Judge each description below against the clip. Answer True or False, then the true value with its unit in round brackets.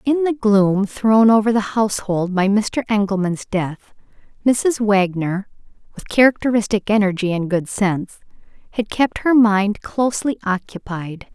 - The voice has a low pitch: False (210 Hz)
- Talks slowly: True (130 wpm)